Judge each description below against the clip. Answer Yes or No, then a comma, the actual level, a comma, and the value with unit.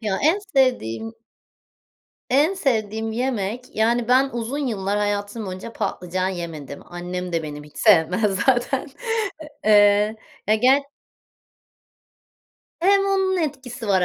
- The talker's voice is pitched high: Yes, high, 220 Hz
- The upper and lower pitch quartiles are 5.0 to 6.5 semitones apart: Yes, wide, 5.4 semitones